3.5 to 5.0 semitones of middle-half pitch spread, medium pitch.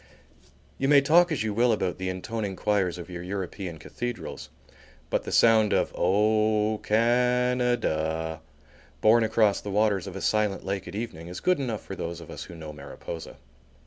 No: average, 4.3 semitones; low, 105 Hz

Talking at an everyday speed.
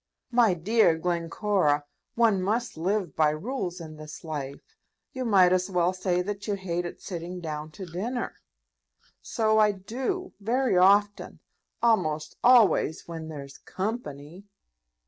No: slow, 130 wpm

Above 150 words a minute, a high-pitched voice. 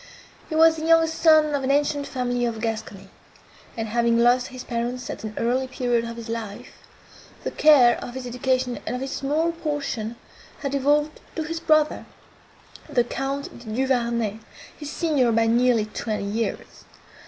Yes: average, 165 wpm; very high, 250 Hz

